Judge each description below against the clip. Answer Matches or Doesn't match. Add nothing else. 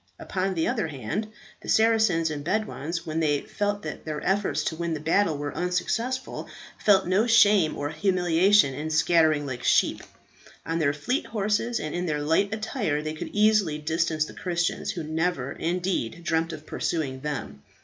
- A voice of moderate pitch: Matches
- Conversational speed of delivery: Matches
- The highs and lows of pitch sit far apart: Doesn't match